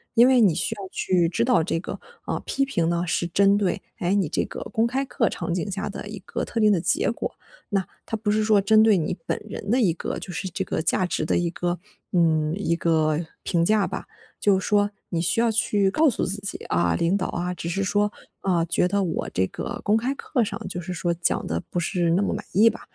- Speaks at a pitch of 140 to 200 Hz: Yes, high, 190 Hz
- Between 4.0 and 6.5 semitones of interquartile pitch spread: No, average, 3.5 semitones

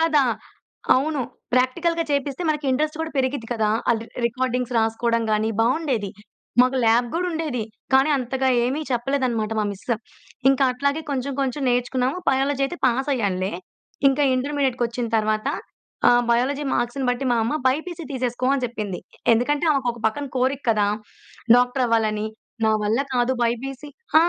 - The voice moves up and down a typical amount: Yes, average, 3.1 semitones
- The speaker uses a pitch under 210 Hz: No, very high, 255 Hz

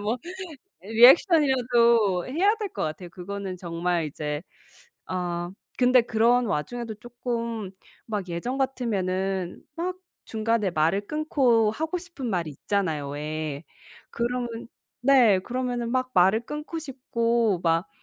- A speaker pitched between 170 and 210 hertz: No, high, 225 Hz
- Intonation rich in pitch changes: Yes, wide, 5.7 semitones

